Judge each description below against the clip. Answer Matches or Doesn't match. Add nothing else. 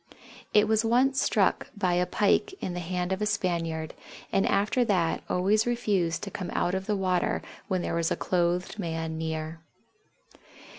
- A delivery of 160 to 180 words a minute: Matches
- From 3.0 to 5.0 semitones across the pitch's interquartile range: Matches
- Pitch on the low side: Doesn't match